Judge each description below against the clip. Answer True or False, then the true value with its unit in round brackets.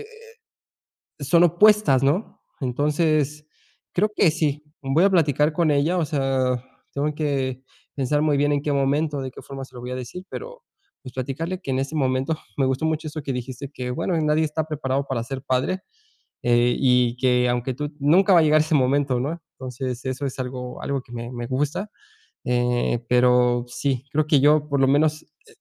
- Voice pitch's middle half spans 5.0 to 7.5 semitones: False (3.2 semitones)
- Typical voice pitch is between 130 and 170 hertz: True (140 Hz)